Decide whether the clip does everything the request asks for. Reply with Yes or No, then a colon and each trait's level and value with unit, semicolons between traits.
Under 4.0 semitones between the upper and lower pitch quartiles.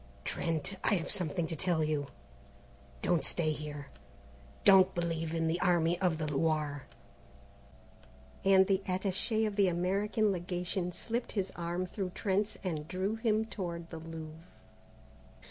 Yes: average, 3.1 semitones